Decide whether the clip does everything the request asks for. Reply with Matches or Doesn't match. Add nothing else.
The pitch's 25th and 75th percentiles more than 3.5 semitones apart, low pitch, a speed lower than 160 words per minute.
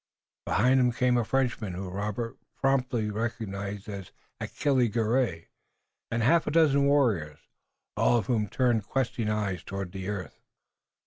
Matches